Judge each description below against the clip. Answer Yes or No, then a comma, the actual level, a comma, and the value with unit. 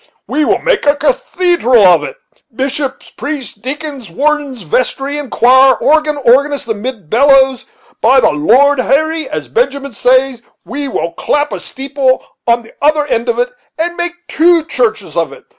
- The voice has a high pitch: Yes, very high, 275 Hz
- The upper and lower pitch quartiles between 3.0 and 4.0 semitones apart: Yes, average, 3.5 semitones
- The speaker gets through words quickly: No, average, 160 wpm